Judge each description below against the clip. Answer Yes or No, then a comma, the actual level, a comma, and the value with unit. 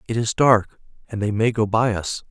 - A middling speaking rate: No, fast, 235 wpm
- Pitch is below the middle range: Yes, low, 110 Hz